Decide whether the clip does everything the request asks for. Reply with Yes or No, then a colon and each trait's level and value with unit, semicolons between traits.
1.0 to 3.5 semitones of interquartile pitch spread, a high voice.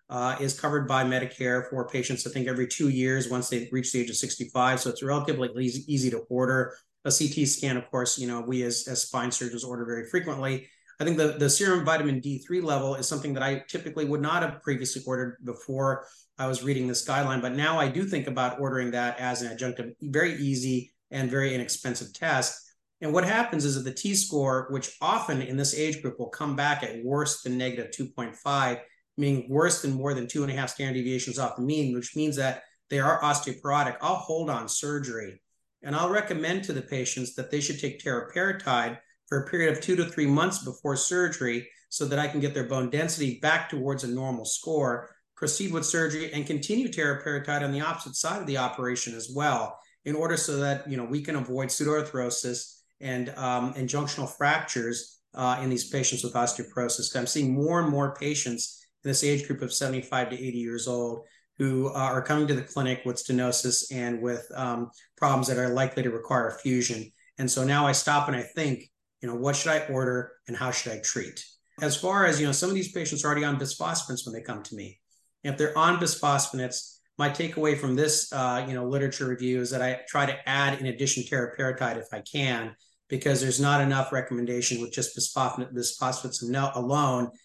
No: average, 2.8 semitones; low, 135 Hz